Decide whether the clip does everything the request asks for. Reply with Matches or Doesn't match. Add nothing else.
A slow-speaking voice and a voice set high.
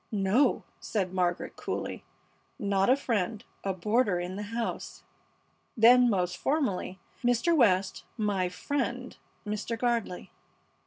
Matches